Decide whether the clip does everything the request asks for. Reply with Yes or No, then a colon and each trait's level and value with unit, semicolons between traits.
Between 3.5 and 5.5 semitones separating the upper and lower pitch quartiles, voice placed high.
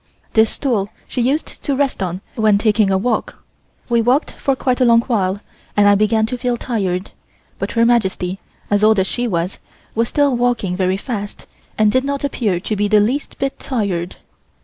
Yes: average, 3.8 semitones; high, 220 Hz